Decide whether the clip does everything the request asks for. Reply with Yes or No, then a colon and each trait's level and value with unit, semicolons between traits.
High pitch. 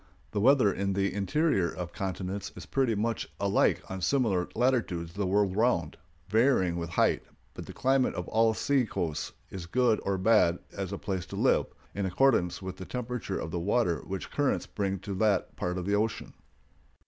No: low, 100 Hz